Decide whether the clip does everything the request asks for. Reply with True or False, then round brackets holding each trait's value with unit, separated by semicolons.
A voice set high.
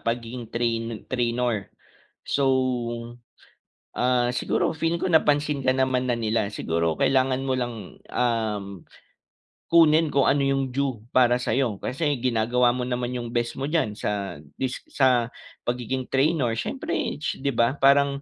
False (125 Hz)